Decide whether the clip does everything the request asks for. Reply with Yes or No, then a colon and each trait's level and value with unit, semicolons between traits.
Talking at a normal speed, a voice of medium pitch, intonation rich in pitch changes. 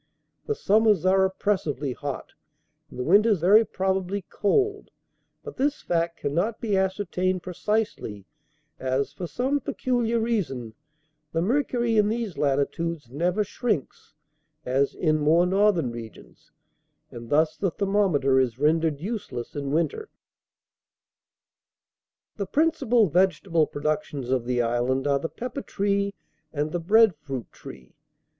No: slow, 130 wpm; medium, 180 Hz; wide, 6.7 semitones